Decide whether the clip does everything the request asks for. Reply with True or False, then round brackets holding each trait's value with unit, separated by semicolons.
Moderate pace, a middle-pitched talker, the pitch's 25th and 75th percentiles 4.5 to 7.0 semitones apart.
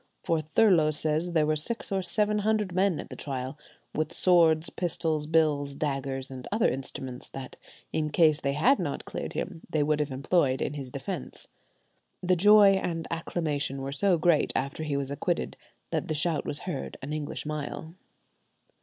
False (175 wpm; 155 Hz; 3.8 semitones)